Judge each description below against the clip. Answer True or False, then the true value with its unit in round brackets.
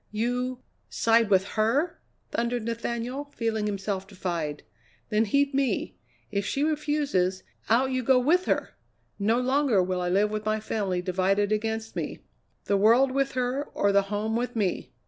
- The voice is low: False (225 Hz)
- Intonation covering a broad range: False (4.3 semitones)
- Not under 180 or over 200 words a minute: False (160 wpm)